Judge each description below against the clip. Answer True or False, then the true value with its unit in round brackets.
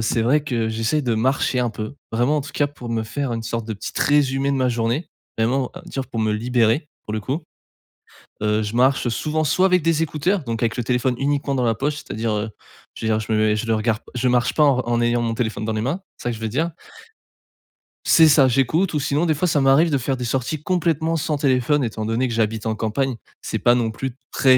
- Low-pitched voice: True (125 Hz)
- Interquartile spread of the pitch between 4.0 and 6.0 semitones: True (4.3 semitones)